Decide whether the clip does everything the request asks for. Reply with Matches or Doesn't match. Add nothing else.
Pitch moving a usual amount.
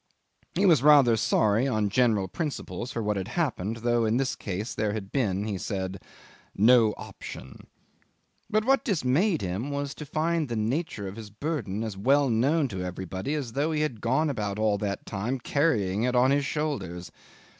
Doesn't match